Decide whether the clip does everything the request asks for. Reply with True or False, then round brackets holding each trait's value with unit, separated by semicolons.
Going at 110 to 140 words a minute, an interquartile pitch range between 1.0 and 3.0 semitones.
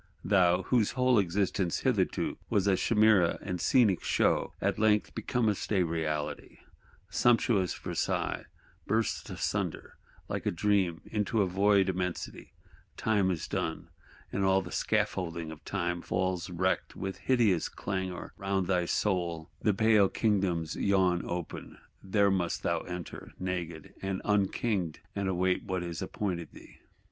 True (135 wpm; 2.7 semitones)